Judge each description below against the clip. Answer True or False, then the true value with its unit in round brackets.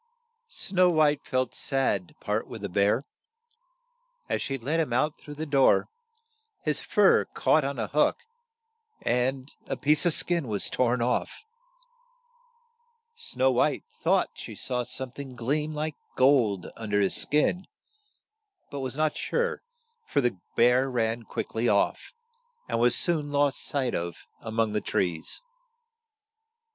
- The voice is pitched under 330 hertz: True (135 Hz)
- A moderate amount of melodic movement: True (4.3 semitones)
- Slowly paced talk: False (150 wpm)